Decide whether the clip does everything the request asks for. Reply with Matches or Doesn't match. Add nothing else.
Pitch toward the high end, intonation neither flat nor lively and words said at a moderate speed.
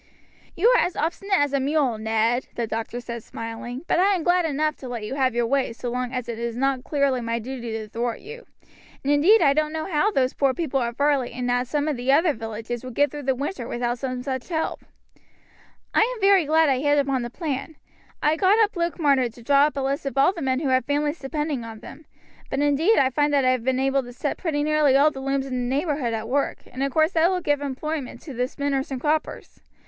Doesn't match